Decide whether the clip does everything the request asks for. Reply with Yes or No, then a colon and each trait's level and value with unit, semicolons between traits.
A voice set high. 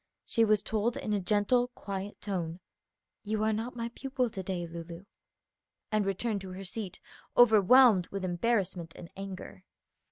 Yes: high, 200 Hz